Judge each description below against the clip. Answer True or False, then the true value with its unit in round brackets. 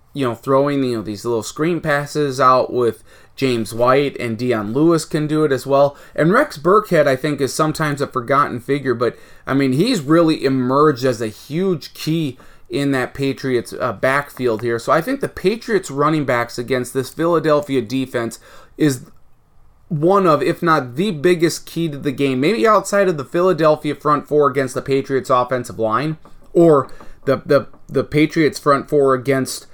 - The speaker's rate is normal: True (180 wpm)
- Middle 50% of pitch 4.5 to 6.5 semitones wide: False (3.3 semitones)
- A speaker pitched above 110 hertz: True (140 Hz)